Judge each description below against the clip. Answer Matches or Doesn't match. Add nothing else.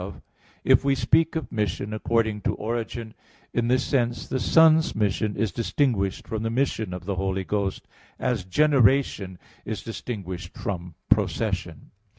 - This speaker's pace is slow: Doesn't match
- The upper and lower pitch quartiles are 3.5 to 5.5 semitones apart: Matches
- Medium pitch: Doesn't match